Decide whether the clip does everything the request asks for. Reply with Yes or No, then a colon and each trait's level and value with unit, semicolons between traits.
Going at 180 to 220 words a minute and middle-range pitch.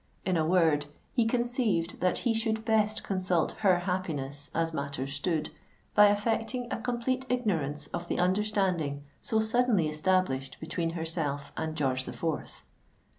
No: average, 145 wpm; medium, 180 Hz